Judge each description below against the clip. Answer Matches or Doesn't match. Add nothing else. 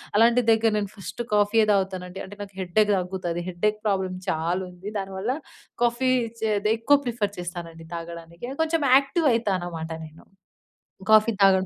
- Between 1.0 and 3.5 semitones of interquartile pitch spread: Doesn't match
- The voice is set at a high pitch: Matches